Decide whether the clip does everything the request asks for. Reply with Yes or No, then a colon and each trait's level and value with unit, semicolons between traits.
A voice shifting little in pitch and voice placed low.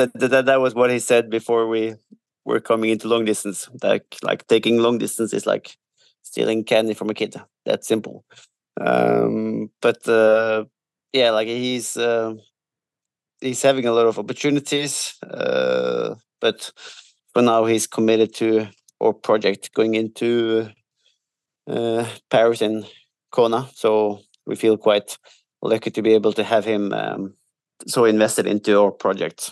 Yes: narrow, 2.1 semitones; low, 115 Hz